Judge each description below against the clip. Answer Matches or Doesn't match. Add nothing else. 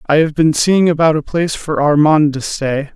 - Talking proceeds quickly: Matches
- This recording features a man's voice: Matches